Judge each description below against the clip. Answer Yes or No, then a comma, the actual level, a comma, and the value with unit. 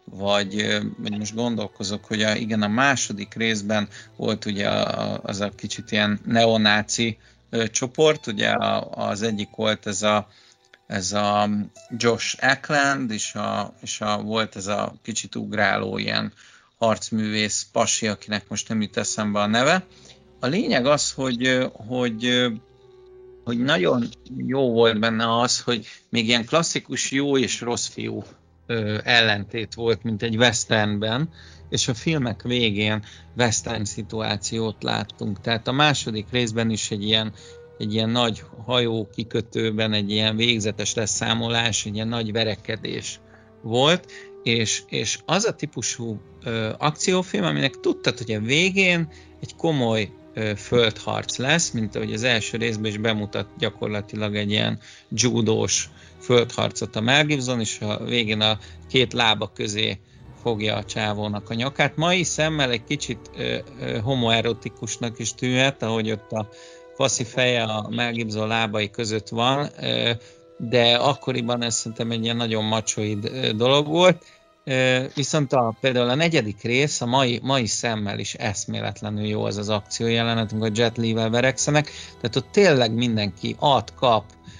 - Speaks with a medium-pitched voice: No, low, 115 Hz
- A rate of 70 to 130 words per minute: No, average, 150 wpm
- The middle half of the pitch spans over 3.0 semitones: No, average, 2.7 semitones